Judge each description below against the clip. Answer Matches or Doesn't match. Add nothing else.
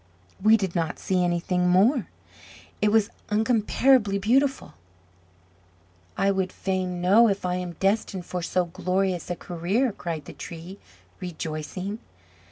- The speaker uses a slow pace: Matches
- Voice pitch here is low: Doesn't match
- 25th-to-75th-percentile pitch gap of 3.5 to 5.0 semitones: Doesn't match